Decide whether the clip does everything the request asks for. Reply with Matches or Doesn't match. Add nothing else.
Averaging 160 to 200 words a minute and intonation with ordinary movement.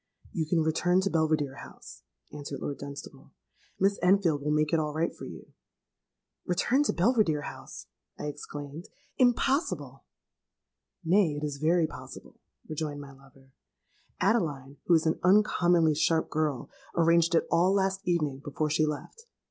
Doesn't match